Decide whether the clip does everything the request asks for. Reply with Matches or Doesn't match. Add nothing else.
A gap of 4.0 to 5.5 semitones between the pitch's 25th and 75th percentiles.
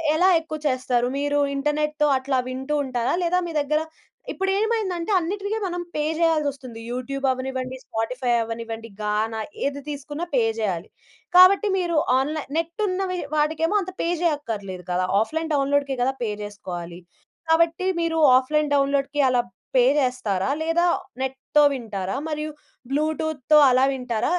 Matches